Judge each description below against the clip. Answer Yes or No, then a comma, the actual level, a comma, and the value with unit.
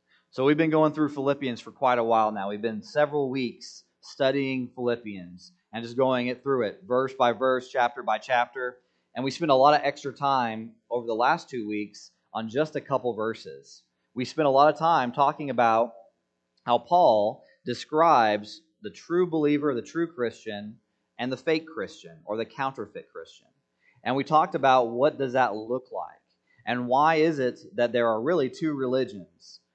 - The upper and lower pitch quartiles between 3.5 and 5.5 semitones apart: Yes, average, 4.1 semitones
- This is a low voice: Yes, low, 125 Hz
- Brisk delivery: No, average, 185 wpm